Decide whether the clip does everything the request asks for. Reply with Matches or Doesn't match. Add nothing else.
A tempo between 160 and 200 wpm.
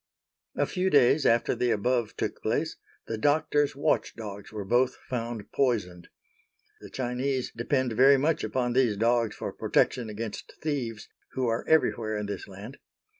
Doesn't match